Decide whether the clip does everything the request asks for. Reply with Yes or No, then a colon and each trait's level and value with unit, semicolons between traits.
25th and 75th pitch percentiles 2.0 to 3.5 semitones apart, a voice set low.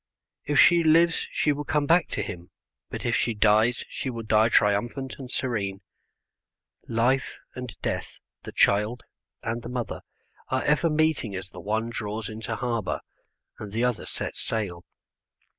No: average, 4.0 semitones; low, 115 Hz